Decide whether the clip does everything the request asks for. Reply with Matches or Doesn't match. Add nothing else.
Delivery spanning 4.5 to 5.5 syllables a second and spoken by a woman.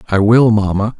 Doesn't match